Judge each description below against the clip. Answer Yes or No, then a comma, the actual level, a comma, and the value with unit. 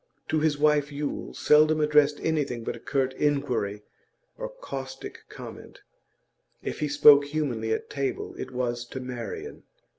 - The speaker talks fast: No, average, 145 wpm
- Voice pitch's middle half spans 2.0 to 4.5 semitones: Yes, average, 2.7 semitones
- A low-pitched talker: No, medium, 145 Hz